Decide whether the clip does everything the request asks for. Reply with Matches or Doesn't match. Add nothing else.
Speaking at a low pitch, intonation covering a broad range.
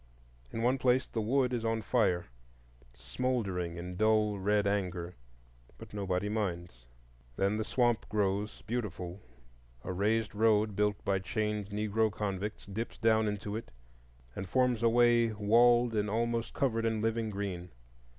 Doesn't match